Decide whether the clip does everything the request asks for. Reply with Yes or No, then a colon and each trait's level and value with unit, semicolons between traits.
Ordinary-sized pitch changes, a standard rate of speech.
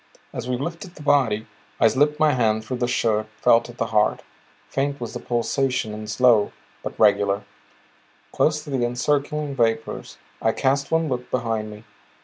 Yes: average, 4.1 semitones; average, 170 wpm